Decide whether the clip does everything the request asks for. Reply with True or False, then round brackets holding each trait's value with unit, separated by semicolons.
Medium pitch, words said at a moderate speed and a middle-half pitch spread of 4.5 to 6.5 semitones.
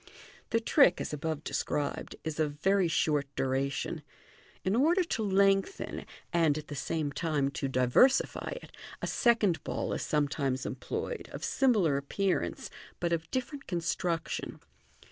True (165 Hz; 150 wpm; 5.5 semitones)